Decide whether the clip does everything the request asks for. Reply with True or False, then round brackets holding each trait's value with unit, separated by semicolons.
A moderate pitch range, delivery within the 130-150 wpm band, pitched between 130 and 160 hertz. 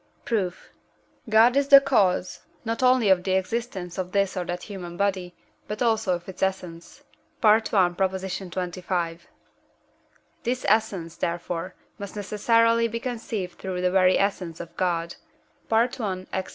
False (3.7 semitones; 140 wpm; 190 Hz)